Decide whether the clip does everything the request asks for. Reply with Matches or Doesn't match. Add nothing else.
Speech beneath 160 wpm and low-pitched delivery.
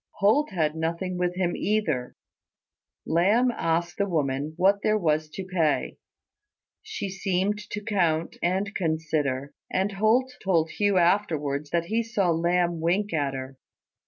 Doesn't match